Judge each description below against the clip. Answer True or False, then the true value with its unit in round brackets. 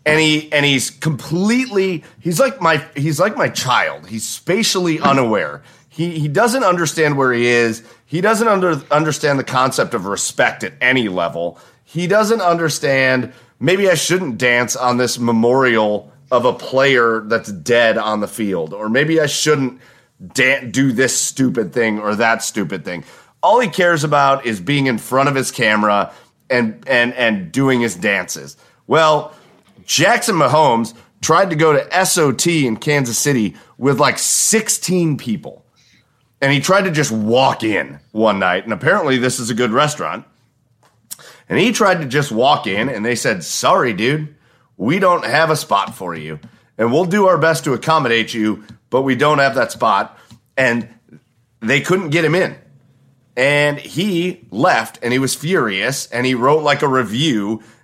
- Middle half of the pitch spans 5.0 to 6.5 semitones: True (5.3 semitones)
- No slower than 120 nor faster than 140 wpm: False (170 wpm)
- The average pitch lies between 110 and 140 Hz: True (135 Hz)